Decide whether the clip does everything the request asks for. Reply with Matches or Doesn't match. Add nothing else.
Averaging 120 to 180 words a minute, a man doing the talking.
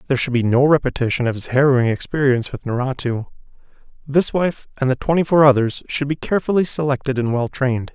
Doesn't match